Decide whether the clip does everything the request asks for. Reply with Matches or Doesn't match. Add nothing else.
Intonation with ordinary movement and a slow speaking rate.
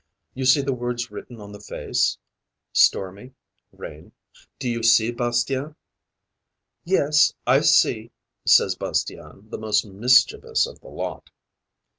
Matches